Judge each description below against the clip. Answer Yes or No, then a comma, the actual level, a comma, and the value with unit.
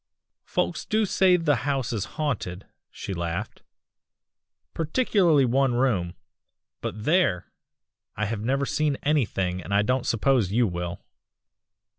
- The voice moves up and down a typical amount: No, wide, 6.9 semitones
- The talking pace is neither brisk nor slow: No, slow, 125 wpm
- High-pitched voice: No, low, 125 Hz